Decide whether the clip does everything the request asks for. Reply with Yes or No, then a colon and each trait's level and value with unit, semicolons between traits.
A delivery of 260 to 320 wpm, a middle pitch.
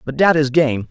Yes: fast, 265 wpm; medium, 145 Hz